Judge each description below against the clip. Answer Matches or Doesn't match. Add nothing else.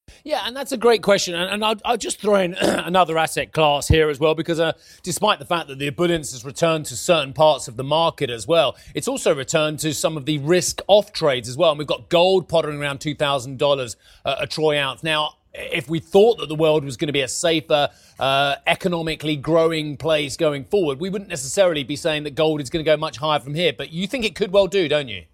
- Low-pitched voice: Doesn't match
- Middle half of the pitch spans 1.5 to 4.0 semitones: Matches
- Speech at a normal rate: Doesn't match